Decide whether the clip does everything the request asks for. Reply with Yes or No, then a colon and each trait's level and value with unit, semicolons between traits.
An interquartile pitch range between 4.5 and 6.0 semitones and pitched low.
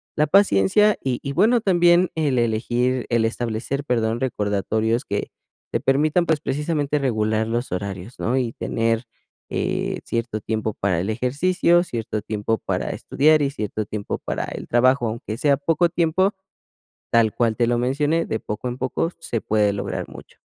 Yes: average, 5.2 semitones; low, 120 Hz